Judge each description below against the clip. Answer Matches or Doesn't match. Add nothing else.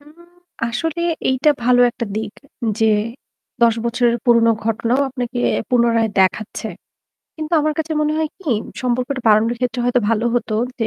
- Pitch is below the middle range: Doesn't match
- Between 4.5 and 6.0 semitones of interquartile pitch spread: Doesn't match